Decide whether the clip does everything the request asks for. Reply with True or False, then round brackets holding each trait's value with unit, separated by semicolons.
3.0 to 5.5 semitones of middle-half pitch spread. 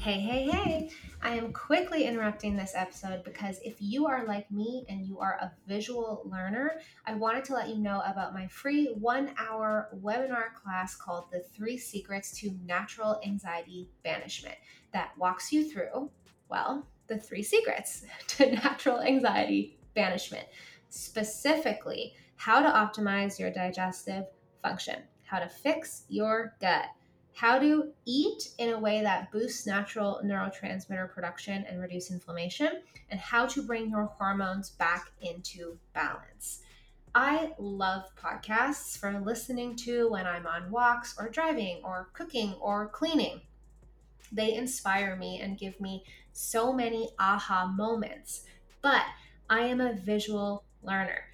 True (4.0 semitones)